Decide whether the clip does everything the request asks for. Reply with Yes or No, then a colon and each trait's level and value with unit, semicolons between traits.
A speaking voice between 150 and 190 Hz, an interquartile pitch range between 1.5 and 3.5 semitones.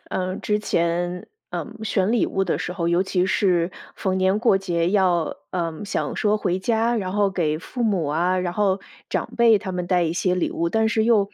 Yes: medium, 185 Hz; average, 3.0 semitones